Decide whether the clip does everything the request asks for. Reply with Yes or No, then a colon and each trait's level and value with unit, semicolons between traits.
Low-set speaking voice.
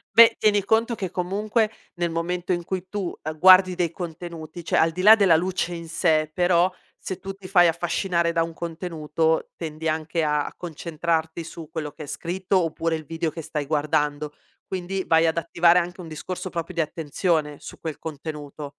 No: medium, 170 Hz